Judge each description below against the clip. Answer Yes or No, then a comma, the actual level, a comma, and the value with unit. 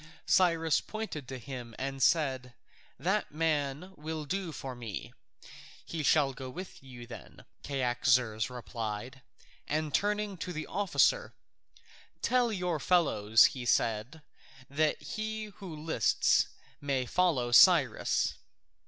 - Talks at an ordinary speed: No, slow, 120 wpm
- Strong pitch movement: Yes, wide, 5.8 semitones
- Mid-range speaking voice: Yes, medium, 145 Hz